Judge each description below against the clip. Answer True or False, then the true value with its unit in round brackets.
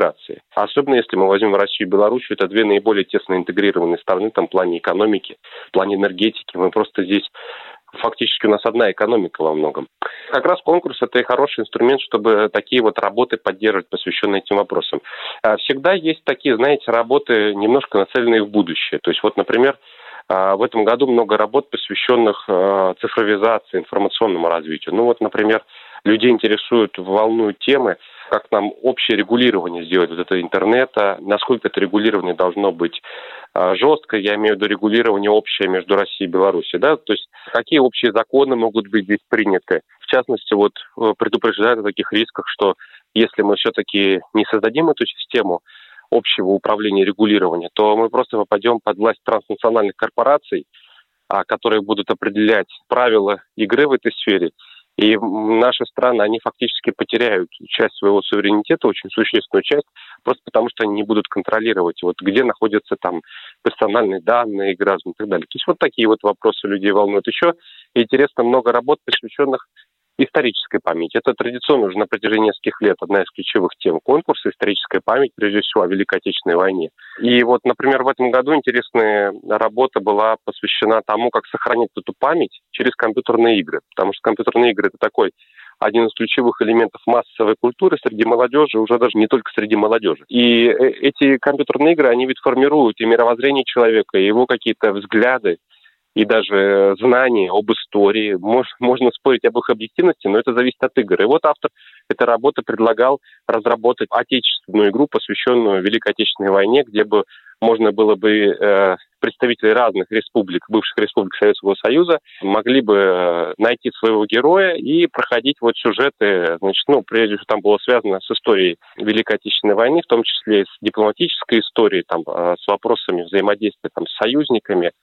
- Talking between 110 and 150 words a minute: False (160 wpm)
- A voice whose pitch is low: True (110 Hz)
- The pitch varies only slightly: False (3.5 semitones)